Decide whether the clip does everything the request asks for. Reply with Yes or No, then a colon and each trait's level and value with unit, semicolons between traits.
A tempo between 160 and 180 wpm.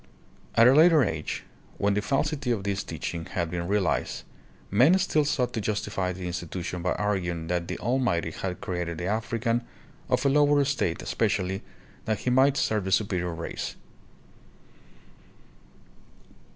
No: average, 150 wpm